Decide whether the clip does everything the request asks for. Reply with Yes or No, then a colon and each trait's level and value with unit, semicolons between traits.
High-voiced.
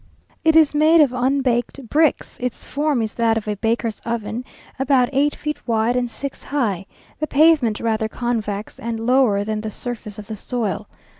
Yes: high, 240 Hz